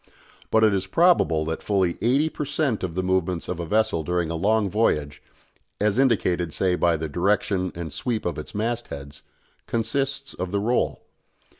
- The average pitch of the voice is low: Yes, very low, 95 Hz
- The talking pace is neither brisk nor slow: Yes, average, 180 wpm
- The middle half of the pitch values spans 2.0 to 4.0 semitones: No, average, 5.0 semitones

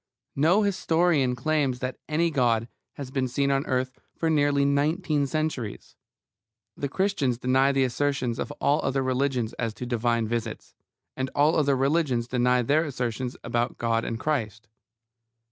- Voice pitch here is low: Yes, low, 130 Hz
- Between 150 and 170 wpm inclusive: Yes, average, 155 wpm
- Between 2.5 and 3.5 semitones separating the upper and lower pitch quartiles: Yes, average, 3.2 semitones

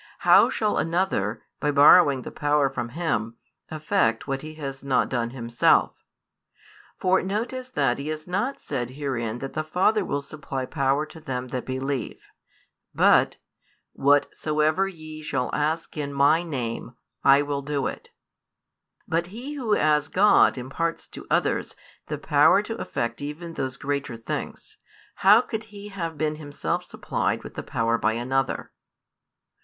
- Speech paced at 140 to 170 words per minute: Yes, average, 150 wpm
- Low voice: No, medium, 145 Hz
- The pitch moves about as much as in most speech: Yes, average, 4.0 semitones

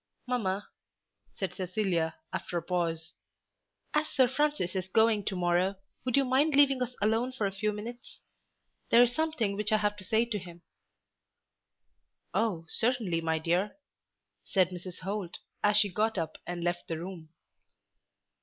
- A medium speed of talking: Yes, average, 155 wpm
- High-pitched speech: Yes, high, 205 Hz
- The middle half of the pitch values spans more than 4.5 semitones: Yes, average, 5.0 semitones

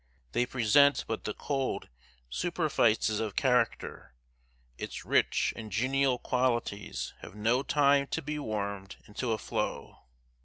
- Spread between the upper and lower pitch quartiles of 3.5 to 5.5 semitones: Yes, average, 4.6 semitones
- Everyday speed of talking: No, slow, 125 wpm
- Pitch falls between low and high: No, low, 120 Hz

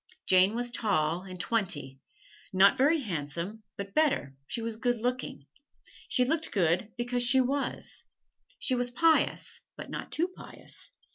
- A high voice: Yes, high, 230 Hz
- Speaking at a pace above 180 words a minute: No, average, 145 wpm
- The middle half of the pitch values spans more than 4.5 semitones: Yes, wide, 5.4 semitones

